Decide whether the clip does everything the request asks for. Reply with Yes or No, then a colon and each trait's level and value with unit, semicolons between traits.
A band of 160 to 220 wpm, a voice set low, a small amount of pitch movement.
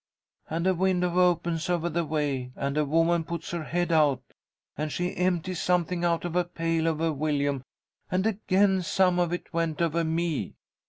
No: average, 175 wpm; medium, 170 Hz; narrow, 2.3 semitones